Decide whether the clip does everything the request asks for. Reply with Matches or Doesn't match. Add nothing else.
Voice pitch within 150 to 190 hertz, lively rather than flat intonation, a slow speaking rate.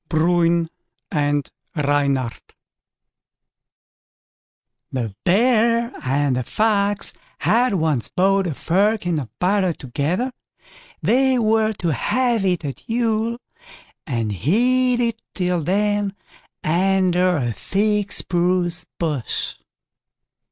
Matches